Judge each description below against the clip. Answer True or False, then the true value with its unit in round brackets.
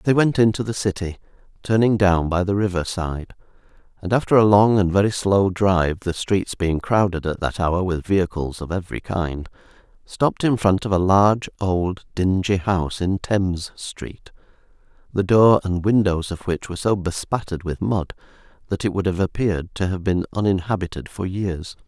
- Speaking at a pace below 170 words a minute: False (180 wpm)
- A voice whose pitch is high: False (95 Hz)